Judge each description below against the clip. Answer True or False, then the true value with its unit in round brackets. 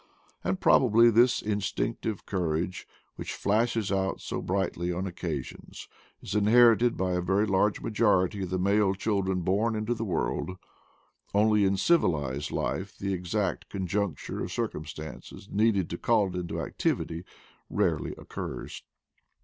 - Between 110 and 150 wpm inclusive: True (140 wpm)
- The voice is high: False (95 Hz)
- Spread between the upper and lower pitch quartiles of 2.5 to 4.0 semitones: True (2.9 semitones)